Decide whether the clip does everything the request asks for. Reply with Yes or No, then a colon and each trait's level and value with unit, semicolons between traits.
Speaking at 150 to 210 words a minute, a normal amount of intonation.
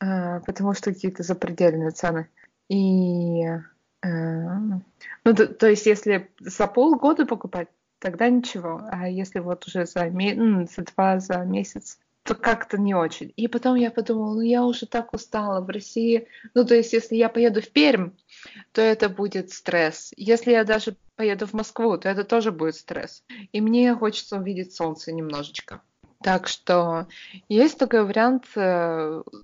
Yes: average, 155 wpm; average, 4.3 semitones